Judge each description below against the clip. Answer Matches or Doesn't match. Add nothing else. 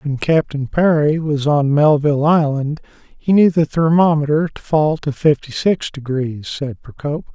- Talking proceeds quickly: Doesn't match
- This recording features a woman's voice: Doesn't match